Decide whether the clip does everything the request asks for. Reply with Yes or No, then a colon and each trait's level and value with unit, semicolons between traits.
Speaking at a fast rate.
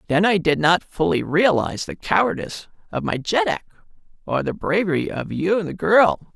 No: average, 180 wpm